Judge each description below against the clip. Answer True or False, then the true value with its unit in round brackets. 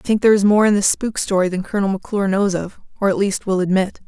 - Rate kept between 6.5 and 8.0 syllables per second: True (7.3 syllables/s)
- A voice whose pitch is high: True (195 Hz)